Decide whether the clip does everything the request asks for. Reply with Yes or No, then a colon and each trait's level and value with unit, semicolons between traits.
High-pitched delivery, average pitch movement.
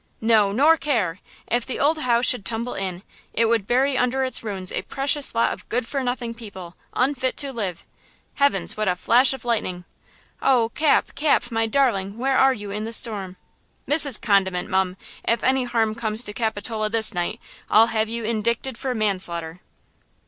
Yes: high, 230 Hz; average, 4.1 semitones